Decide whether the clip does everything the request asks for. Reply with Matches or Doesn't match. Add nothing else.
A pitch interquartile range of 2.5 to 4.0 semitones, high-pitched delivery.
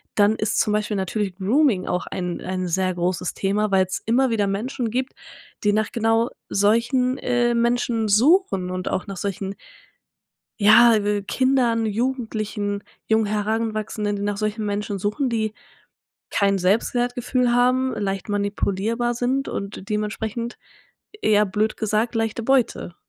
Matches